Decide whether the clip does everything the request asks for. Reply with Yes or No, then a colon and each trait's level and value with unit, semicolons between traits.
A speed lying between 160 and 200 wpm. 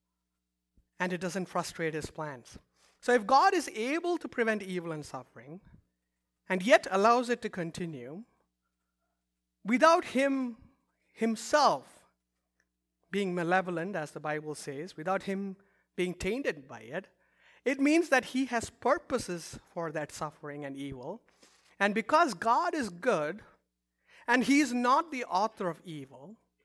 No: slow, 135 wpm